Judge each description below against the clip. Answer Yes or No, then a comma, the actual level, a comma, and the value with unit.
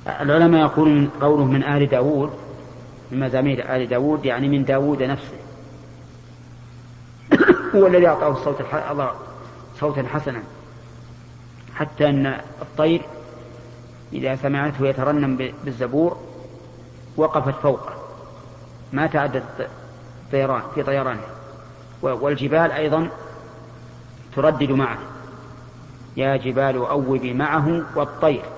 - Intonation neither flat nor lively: Yes, average, 3.0 semitones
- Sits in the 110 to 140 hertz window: Yes, low, 135 Hz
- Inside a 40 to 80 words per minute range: No, average, 90 wpm